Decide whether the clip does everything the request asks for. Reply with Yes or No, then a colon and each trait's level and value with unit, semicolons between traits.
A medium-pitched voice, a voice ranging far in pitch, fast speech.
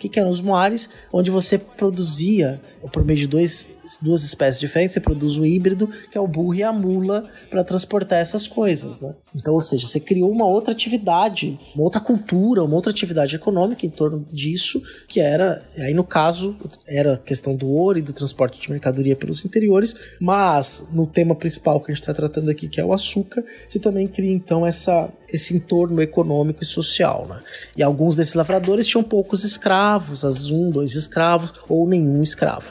No: medium, 170 Hz; average, 4.5 semitones; fast, 190 wpm